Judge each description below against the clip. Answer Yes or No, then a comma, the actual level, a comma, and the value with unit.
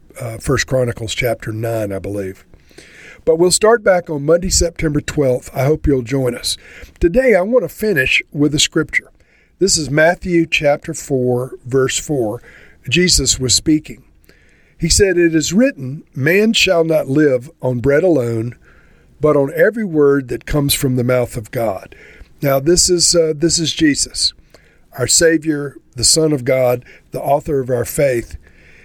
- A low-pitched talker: No, medium, 145 Hz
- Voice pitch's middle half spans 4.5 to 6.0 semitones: Yes, average, 4.9 semitones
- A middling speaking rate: Yes, average, 165 wpm